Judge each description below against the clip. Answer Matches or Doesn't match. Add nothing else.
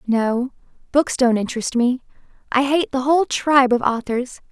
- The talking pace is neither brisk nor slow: Matches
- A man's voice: Doesn't match